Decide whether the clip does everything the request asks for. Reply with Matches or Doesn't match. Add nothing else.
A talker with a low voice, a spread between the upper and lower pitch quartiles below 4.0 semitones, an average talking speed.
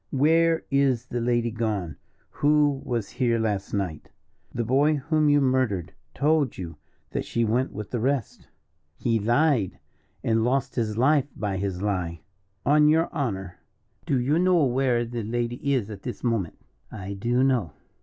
Doesn't match